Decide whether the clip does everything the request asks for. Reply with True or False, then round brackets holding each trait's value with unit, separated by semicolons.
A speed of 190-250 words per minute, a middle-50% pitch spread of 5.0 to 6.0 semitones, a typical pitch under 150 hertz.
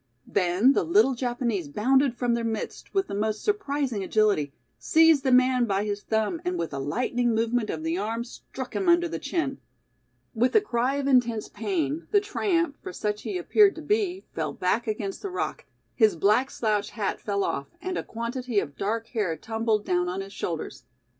False (195 wpm; 5.4 semitones; 235 Hz)